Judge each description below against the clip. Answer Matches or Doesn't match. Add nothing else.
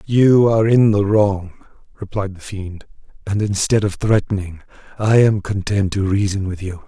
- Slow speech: Doesn't match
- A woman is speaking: Doesn't match